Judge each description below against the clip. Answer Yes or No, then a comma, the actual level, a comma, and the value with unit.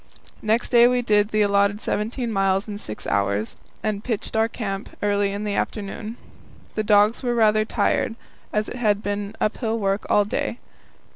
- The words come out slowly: No, average, 170 wpm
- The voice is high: Yes, high, 210 Hz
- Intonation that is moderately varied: No, narrow, 1.7 semitones